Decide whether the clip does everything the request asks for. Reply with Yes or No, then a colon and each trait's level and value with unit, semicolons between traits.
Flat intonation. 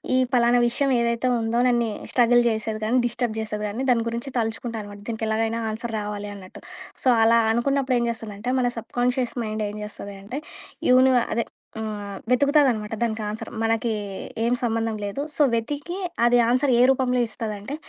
Yes: narrow, 2.2 semitones